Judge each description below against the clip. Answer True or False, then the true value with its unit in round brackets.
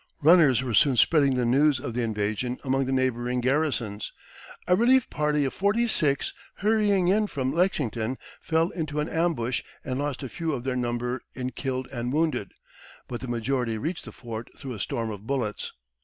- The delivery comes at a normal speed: True (185 wpm)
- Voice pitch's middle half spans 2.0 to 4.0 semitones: False (4.4 semitones)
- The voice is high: False (130 Hz)